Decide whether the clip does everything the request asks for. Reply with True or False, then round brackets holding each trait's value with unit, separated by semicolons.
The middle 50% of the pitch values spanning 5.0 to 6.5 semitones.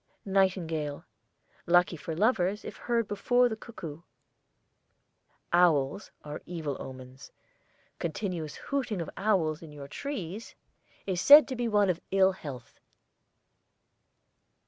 True (5.3 semitones)